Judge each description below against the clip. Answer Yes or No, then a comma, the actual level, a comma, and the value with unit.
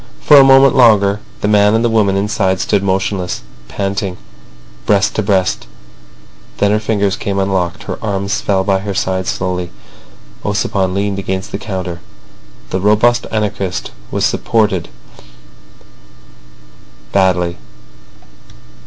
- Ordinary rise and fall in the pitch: No, narrow, 2.0 semitones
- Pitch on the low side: Yes, low, 100 Hz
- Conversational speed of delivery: No, slow, 125 wpm